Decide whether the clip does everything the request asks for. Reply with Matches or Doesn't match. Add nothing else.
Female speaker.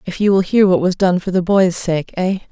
Matches